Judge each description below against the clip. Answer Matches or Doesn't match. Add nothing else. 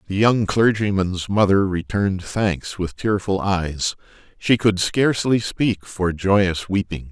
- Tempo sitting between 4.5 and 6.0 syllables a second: Doesn't match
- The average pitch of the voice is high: Doesn't match